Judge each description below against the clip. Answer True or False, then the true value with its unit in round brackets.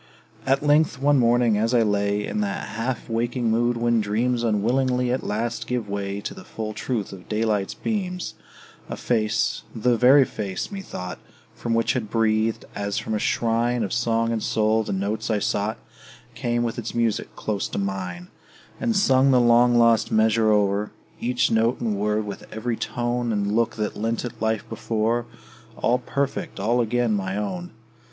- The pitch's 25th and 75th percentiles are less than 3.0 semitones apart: True (2.4 semitones)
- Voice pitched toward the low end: True (115 Hz)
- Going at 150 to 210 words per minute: True (175 wpm)